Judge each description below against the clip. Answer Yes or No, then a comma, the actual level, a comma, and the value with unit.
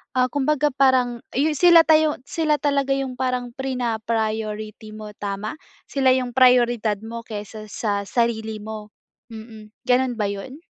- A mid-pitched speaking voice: No, high, 240 Hz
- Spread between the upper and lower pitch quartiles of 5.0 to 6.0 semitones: No, average, 3.6 semitones